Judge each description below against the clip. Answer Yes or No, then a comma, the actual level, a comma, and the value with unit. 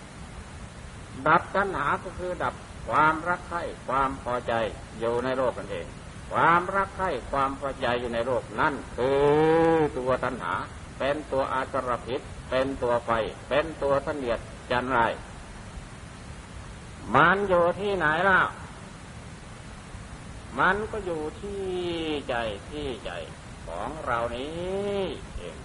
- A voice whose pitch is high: No, medium, 140 Hz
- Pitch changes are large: Yes, wide, 6.0 semitones